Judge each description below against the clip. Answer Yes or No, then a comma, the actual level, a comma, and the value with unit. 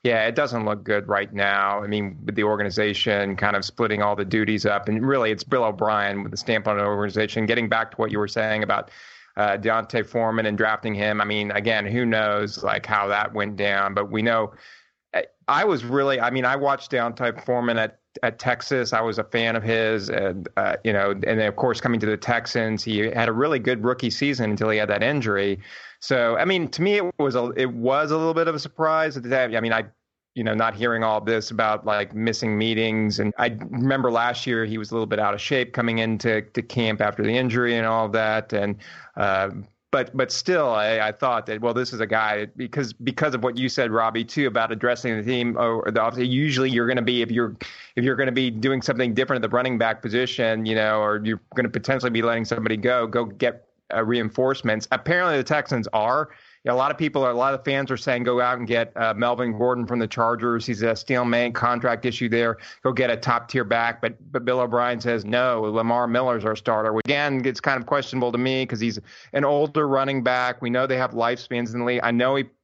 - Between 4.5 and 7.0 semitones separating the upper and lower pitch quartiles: No, narrow, 2.6 semitones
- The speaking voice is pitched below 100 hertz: No, low, 115 Hz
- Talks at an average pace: No, fast, 240 wpm